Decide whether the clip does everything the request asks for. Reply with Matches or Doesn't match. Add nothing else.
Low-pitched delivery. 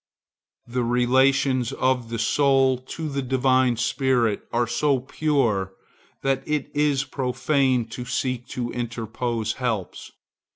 Matches